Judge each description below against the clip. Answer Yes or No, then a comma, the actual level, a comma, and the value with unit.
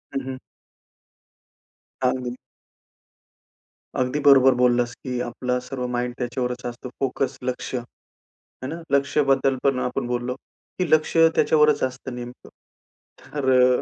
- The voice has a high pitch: No, low, 125 Hz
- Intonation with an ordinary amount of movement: No, narrow, 1.7 semitones